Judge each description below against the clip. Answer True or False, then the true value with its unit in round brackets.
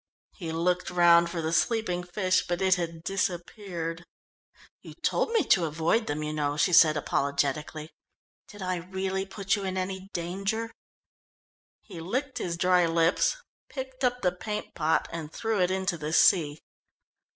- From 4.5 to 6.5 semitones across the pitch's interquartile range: False (2.8 semitones)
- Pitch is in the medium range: True (180 Hz)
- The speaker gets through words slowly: False (160 wpm)